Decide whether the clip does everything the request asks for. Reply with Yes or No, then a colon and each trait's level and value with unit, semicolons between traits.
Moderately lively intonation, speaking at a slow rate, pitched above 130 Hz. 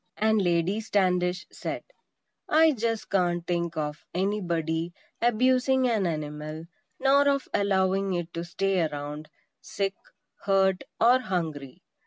Yes: average, 4.6 semitones; slow, 120 wpm; high, 190 Hz